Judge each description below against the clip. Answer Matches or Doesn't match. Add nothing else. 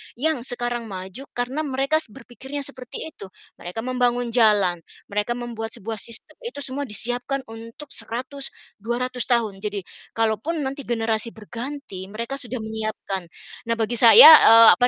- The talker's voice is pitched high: Matches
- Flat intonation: Doesn't match